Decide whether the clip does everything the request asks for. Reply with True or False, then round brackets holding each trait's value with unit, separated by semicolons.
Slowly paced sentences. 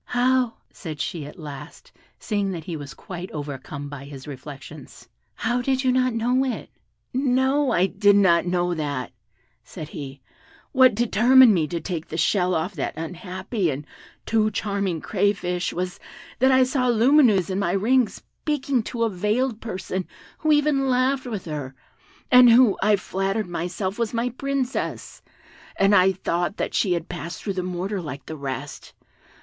False (165 wpm)